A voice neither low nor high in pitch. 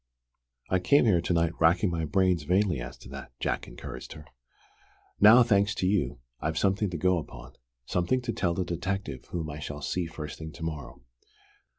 No: very low, 85 Hz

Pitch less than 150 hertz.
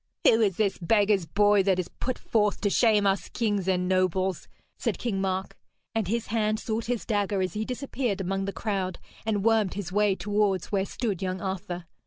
No: high, 200 Hz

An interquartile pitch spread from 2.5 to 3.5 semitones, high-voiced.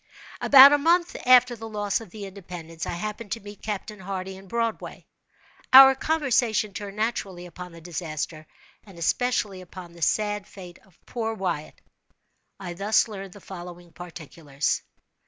No: average, 4.2 semitones; high, 195 Hz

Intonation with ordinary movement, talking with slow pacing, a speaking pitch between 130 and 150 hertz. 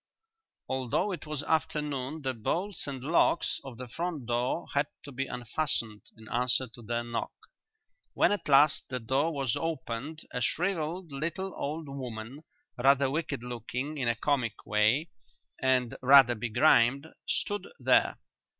No: average, 4.2 semitones; average, 145 wpm; low, 135 Hz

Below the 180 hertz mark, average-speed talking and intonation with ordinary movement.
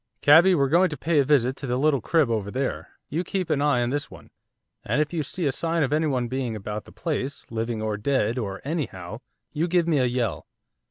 No: medium, 140 Hz; fast, 230 wpm; average, 4.7 semitones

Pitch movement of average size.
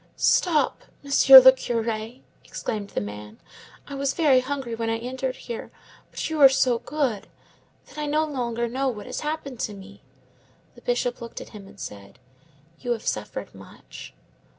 Yes: average, 3.9 semitones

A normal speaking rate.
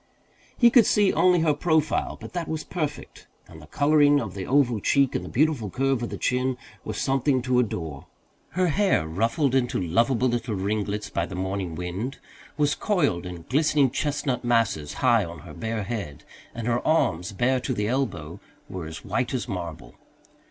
Yes: average, 180 wpm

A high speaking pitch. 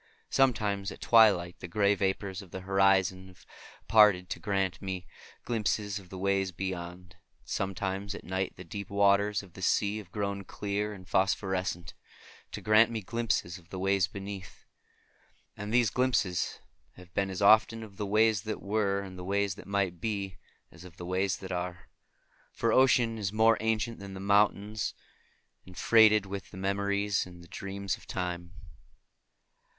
No: low, 100 Hz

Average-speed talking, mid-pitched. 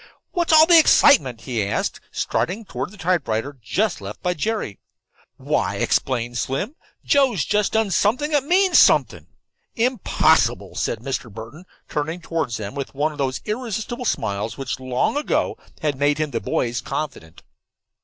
Yes: average, 155 wpm; medium, 155 Hz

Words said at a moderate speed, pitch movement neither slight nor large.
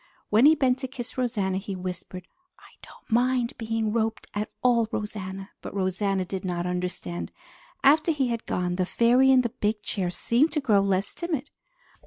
Yes: average, 180 wpm; average, 4.9 semitones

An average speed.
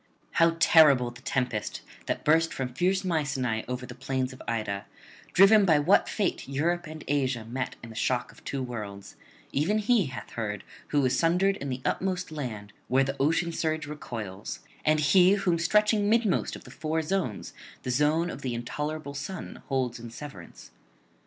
Yes: average, 175 wpm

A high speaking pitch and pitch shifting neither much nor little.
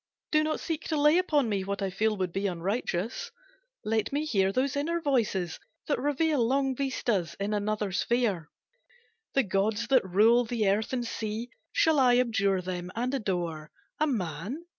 No: high, 225 Hz; wide, 5.8 semitones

